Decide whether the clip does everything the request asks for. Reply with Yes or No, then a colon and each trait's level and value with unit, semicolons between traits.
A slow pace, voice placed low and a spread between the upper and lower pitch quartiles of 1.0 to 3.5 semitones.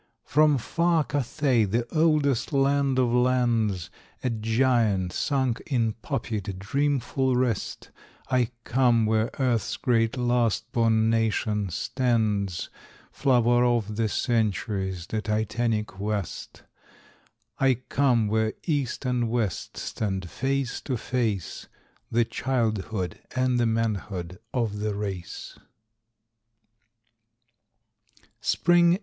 Yes: slow, 100 wpm; low, 115 Hz; average, 3.2 semitones